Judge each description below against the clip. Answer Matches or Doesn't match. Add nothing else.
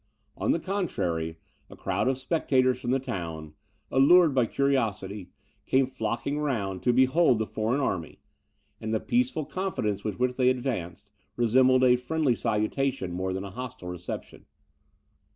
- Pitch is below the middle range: Matches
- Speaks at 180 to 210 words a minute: Doesn't match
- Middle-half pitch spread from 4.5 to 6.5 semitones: Matches